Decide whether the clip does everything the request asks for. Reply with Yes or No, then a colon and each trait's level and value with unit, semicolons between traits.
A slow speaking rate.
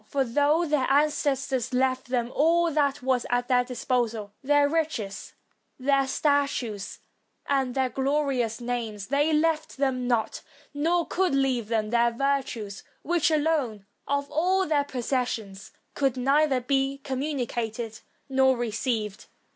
Yes: slow, 130 wpm